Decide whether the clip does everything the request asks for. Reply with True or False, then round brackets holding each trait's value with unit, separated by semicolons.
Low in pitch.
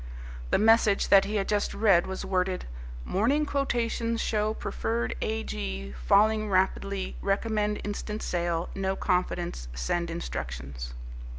False (195 Hz)